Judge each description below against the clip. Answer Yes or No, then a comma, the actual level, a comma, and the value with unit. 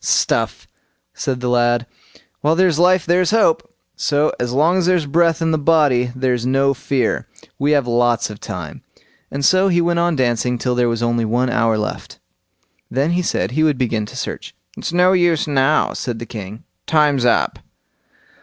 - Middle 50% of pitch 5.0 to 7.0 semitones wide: Yes, average, 5.3 semitones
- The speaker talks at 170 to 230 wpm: Yes, average, 180 wpm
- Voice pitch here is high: No, medium, 140 Hz